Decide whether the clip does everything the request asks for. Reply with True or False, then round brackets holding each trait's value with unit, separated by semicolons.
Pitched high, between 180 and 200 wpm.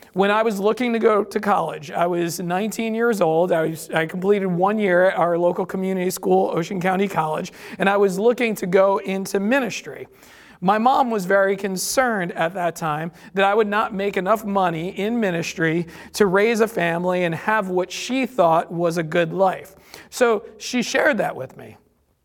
True (195 Hz; 190 wpm)